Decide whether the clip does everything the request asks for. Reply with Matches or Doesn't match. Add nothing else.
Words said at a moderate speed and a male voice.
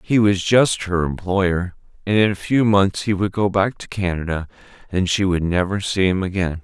Doesn't match